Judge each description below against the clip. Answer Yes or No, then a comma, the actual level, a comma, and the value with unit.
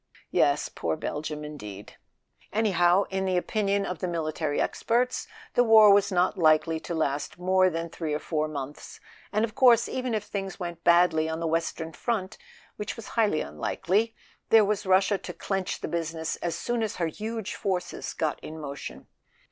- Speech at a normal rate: Yes, average, 180 wpm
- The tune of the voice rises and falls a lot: No, average, 4.6 semitones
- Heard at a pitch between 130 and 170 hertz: No, medium, 180 Hz